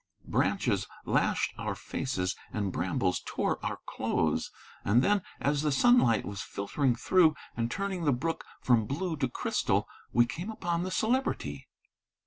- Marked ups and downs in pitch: Yes, wide, 7.7 semitones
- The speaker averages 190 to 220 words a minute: No, average, 145 wpm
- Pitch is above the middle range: No, medium, 140 Hz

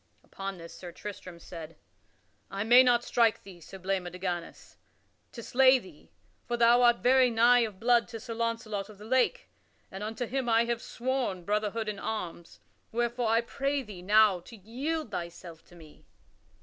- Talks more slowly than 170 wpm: No, average, 175 wpm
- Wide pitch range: No, average, 4.1 semitones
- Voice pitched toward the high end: Yes, high, 220 Hz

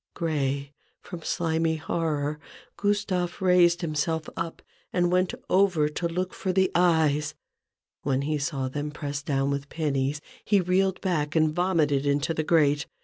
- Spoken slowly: No, average, 150 wpm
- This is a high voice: No, medium, 160 Hz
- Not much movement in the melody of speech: No, average, 3.4 semitones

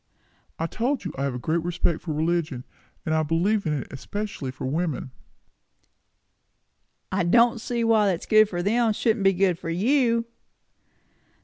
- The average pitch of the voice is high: No, medium, 180 Hz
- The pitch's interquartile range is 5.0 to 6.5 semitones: Yes, wide, 5.5 semitones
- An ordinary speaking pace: Yes, average, 165 wpm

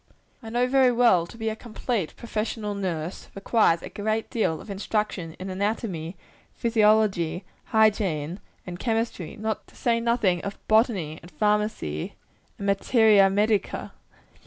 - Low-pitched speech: No, high, 210 Hz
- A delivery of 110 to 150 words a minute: Yes, slow, 135 wpm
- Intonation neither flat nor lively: Yes, average, 3.5 semitones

